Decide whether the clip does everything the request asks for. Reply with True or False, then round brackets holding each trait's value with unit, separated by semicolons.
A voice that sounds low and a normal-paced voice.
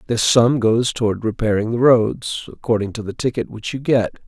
True (115 Hz; 195 wpm)